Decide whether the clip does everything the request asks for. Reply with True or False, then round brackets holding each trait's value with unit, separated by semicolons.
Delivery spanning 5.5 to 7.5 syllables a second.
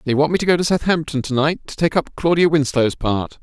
True (5.8 syllables/s)